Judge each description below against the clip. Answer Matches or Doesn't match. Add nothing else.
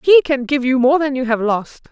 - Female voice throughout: Matches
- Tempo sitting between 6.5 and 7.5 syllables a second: Doesn't match